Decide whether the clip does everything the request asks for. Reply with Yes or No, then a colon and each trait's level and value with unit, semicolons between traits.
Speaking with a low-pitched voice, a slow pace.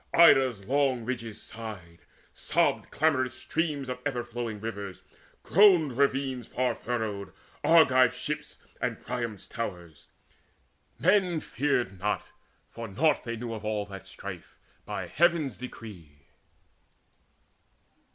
Yes: low, 120 Hz; slow, 115 wpm